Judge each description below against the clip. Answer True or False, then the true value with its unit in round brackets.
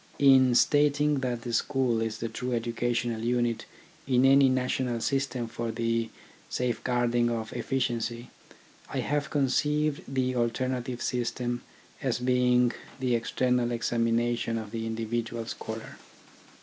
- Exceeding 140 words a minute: False (135 wpm)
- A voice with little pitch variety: True (1.8 semitones)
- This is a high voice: False (120 Hz)